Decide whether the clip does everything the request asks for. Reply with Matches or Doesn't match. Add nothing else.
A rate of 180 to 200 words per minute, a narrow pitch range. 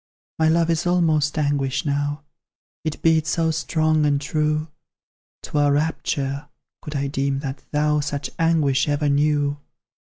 Doesn't match